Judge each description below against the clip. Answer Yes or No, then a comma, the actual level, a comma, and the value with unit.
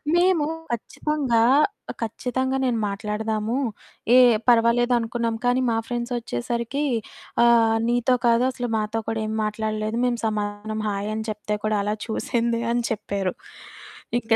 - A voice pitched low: No, high, 230 Hz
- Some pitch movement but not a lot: No, narrow, 2.0 semitones